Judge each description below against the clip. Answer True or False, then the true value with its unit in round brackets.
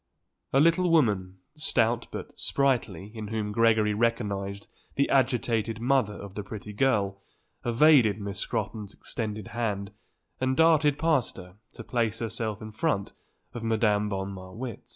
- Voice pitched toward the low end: True (110 Hz)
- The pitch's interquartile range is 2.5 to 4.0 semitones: True (3.6 semitones)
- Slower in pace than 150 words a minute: True (140 wpm)